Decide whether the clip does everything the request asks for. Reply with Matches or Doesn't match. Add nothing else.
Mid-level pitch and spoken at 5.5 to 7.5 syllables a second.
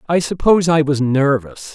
Doesn't match